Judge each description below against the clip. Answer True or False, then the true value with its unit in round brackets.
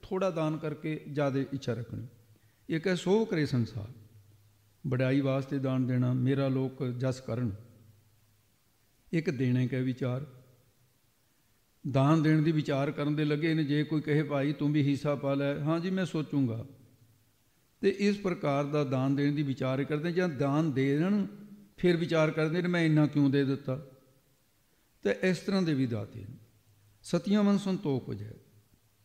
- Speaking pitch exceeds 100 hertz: True (140 Hz)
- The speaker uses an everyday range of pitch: True (4.3 semitones)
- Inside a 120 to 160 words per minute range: True (155 wpm)